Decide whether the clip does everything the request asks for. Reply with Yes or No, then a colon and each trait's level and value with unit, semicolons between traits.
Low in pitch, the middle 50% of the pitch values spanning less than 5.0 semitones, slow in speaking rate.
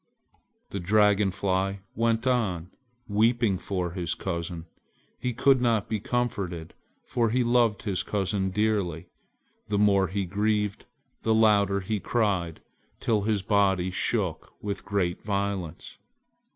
Yes: low, 100 Hz; average, 2.7 semitones; slow, 125 wpm